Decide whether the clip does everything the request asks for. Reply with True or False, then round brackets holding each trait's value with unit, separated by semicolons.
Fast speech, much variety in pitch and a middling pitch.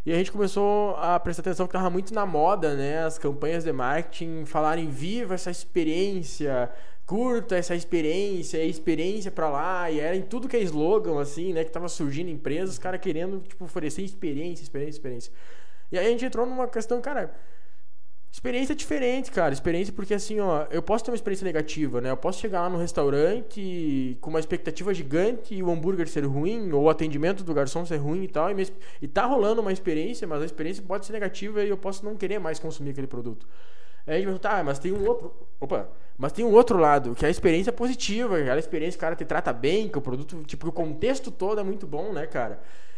False (215 wpm; 4.5 semitones; 175 Hz)